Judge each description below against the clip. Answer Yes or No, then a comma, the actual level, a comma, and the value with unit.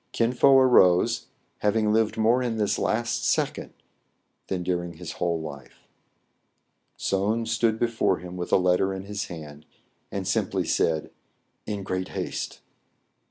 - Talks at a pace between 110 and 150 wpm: Yes, average, 140 wpm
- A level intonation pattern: No, average, 4.0 semitones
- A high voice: No, very low, 95 Hz